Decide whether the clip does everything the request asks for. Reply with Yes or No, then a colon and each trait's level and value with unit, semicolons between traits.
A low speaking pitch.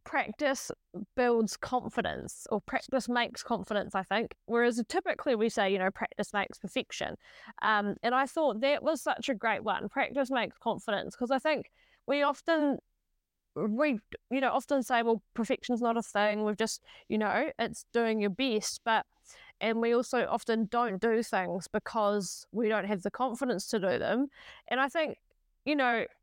No: high, 235 Hz